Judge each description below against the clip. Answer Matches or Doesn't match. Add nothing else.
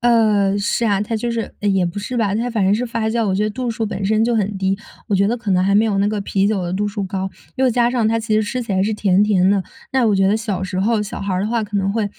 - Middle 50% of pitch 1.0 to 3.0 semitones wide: Matches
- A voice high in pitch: Matches